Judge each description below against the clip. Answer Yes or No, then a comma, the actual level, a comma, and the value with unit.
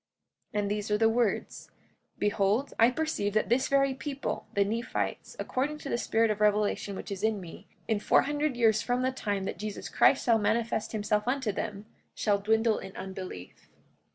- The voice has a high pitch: Yes, high, 220 Hz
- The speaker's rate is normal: Yes, average, 185 wpm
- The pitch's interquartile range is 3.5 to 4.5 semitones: No, average, 3.1 semitones